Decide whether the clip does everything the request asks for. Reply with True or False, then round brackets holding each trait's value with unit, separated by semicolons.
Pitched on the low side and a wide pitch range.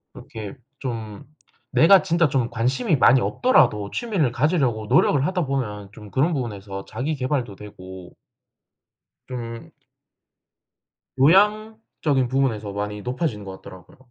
True (125 Hz; 6.3 semitones)